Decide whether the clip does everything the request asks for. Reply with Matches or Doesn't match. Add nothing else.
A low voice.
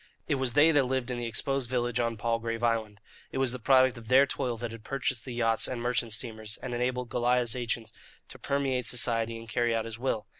Matches